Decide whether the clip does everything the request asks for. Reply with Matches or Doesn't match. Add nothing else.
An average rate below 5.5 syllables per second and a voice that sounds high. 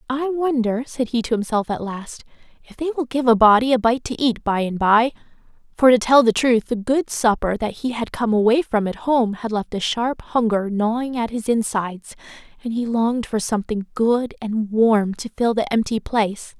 Matches